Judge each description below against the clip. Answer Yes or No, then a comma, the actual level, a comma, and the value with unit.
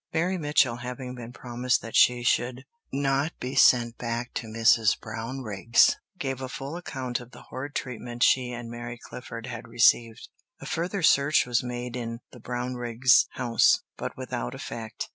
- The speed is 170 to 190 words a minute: No, average, 160 wpm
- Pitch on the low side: Yes, low, 125 Hz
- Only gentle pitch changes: Yes, narrow, 1.9 semitones